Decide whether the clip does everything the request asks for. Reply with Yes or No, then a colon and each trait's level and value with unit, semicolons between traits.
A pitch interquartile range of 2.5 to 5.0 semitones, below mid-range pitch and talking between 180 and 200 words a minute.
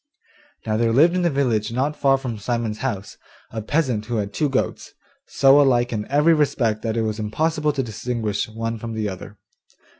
Yes: average, 4.2 semitones; low, 120 Hz; average, 190 wpm